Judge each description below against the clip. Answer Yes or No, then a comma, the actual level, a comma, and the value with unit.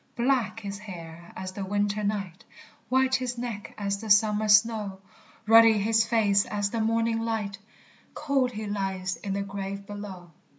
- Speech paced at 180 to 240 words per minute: No, average, 165 wpm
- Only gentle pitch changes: Yes, narrow, 2.2 semitones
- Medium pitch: No, high, 210 Hz